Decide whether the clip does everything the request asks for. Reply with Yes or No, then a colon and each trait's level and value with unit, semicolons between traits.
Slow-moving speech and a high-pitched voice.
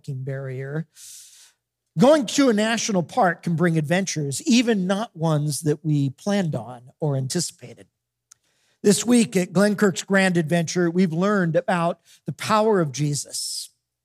No: slow, 130 wpm; medium, 170 Hz